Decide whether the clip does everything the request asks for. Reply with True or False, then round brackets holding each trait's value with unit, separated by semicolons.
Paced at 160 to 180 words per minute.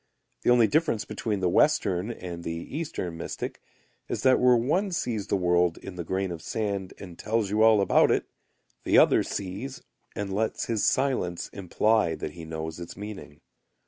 True (175 wpm)